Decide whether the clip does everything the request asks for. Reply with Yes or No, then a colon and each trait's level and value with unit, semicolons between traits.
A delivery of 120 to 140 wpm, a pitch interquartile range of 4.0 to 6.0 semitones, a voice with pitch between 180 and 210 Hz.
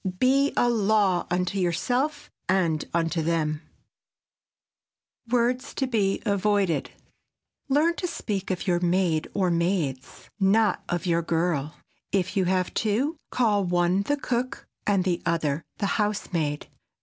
Yes: slow, 135 wpm; average, 4.3 semitones; high, 190 Hz